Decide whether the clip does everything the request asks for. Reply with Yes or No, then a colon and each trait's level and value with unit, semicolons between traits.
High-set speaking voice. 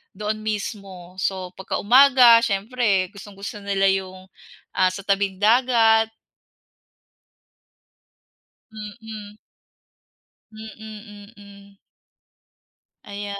Yes: high, 205 Hz